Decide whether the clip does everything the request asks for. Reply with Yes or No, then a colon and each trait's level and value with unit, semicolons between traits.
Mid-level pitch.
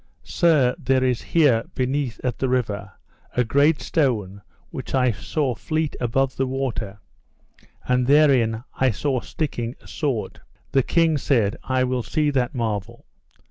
No: low, 130 Hz